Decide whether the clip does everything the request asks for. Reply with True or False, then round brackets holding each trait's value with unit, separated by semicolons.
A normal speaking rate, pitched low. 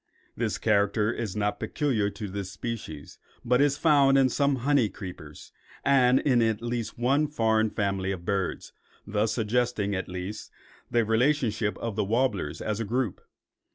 True (155 wpm; 110 Hz)